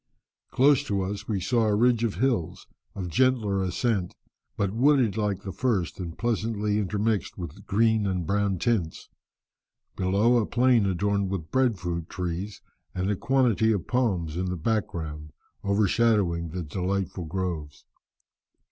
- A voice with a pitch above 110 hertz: No, low, 100 Hz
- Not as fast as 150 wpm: Yes, average, 140 wpm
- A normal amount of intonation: Yes, average, 3.8 semitones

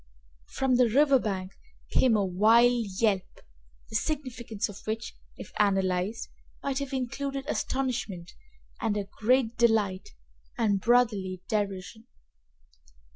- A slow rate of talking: Yes, slow, 110 wpm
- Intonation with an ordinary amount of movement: Yes, average, 4.1 semitones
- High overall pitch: Yes, high, 225 Hz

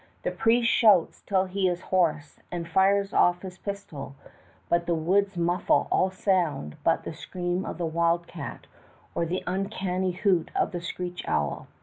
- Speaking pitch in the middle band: Yes, medium, 180 Hz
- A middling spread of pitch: No, narrow, 2.1 semitones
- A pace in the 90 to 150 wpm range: No, average, 165 wpm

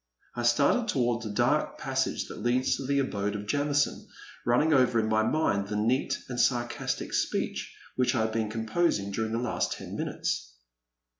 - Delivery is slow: No, average, 175 wpm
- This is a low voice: Yes, low, 120 Hz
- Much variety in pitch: No, average, 3.5 semitones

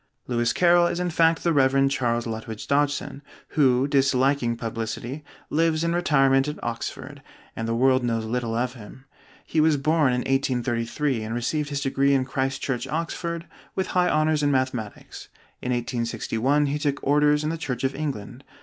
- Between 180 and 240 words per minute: No, average, 170 wpm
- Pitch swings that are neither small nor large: Yes, average, 3.7 semitones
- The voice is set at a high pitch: No, low, 135 Hz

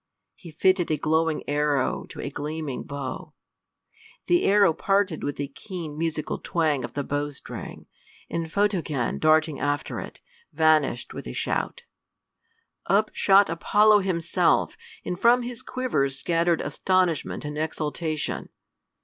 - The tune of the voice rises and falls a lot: No, average, 4.3 semitones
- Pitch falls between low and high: Yes, medium, 160 Hz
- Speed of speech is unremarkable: No, slow, 130 wpm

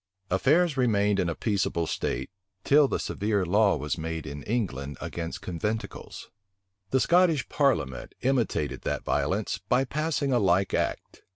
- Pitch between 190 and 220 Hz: No, low, 105 Hz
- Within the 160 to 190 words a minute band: No, average, 145 wpm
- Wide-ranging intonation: Yes, wide, 7.8 semitones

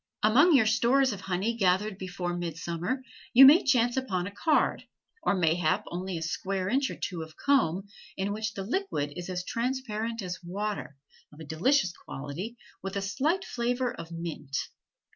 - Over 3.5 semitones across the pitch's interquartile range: Yes, wide, 5.6 semitones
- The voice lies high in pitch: Yes, high, 195 Hz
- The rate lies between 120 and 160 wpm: No, average, 170 wpm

